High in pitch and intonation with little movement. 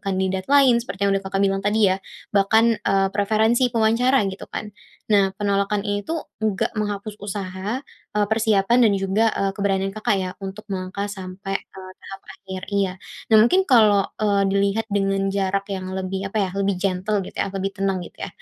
Yes: high, 200 Hz; narrow, 1.7 semitones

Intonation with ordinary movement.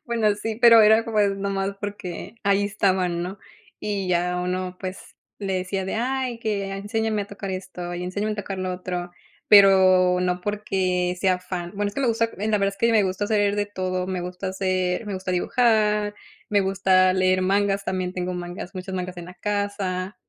No: narrow, 2.1 semitones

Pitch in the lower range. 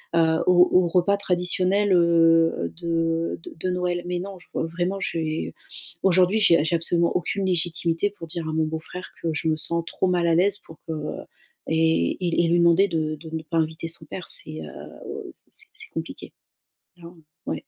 No: medium, 170 Hz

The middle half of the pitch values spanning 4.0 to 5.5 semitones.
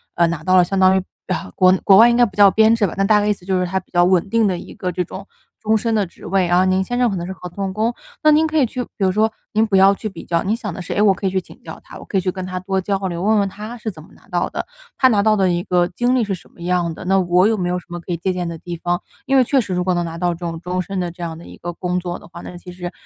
No: average, 2.9 semitones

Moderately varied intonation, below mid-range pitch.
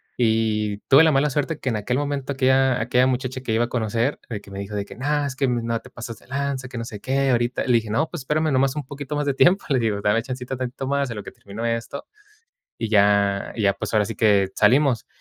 Yes: average, 3.6 semitones; low, 125 Hz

